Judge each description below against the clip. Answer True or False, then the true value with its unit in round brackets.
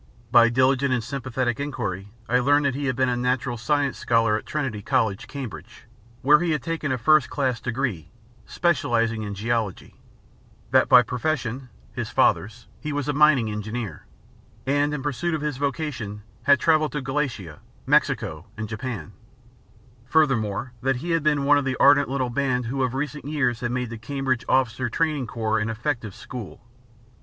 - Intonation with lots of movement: False (3.7 semitones)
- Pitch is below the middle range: True (130 Hz)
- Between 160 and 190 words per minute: True (170 wpm)